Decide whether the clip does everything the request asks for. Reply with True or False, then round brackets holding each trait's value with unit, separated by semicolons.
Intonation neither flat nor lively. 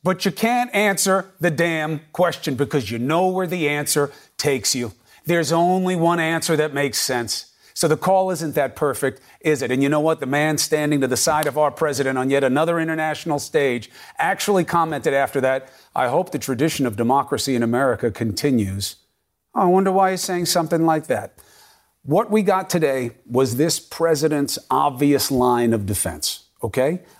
True (4.4 semitones)